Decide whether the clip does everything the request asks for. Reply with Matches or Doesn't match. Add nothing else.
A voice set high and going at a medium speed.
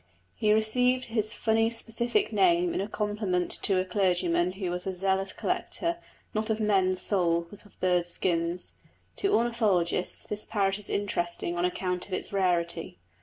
Matches